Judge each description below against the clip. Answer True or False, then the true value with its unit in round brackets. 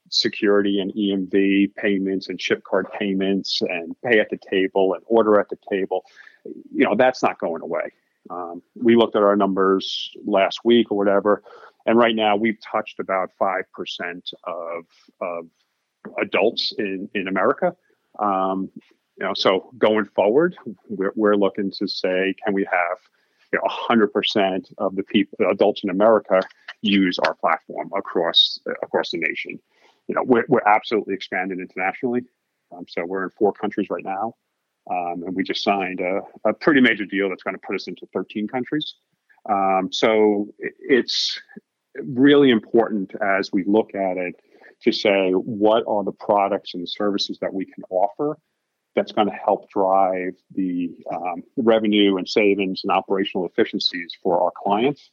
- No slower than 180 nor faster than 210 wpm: False (165 wpm)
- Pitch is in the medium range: False (100 Hz)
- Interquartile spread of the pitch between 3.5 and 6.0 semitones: False (2.7 semitones)